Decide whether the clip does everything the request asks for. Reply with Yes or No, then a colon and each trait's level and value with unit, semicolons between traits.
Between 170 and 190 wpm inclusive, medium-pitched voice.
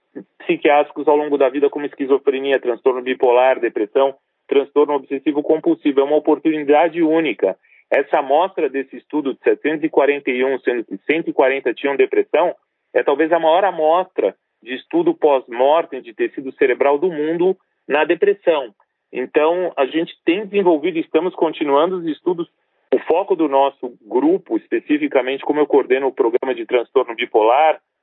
No: average, 145 wpm; medium, 165 Hz